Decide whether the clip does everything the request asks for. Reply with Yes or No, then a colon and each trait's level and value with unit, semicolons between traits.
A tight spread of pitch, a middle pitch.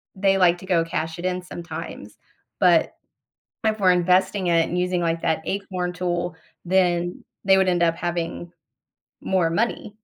Yes: narrow, 1.6 semitones; medium, 180 Hz